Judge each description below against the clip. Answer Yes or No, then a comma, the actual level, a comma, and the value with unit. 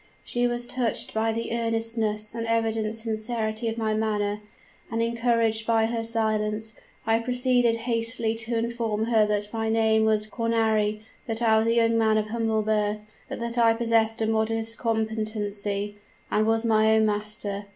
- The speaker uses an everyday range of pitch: No, narrow, 1.0 semitones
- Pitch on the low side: No, high, 225 Hz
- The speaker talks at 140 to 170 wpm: Yes, average, 165 wpm